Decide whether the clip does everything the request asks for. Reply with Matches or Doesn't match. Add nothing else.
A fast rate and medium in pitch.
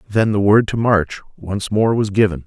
Doesn't match